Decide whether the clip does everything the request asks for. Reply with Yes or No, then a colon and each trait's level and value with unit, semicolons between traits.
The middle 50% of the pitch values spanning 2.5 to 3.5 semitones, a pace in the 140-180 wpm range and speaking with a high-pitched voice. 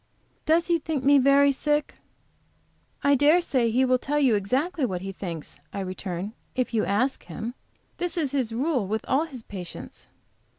No: wide, 5.5 semitones; average, 175 wpm; very high, 260 Hz